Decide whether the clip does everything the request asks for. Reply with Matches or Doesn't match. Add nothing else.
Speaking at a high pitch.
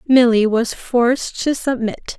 Matches